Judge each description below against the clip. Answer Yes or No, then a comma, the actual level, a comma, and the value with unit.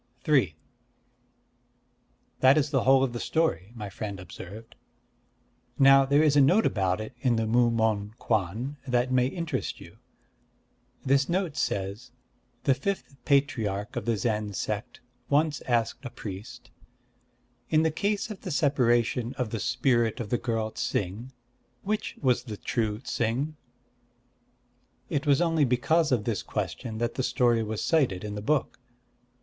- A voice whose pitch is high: No, low, 120 Hz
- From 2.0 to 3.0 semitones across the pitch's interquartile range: No, average, 4.5 semitones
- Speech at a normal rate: Yes, average, 150 wpm